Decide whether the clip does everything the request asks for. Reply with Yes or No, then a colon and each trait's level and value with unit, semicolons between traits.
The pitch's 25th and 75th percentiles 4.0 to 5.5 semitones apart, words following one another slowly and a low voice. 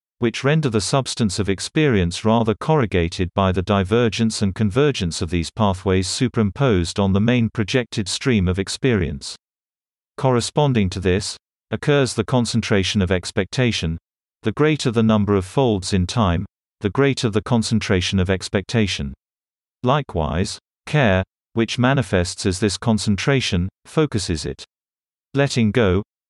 Yes: average, 4.4 semitones; slow, 130 wpm; low, 105 Hz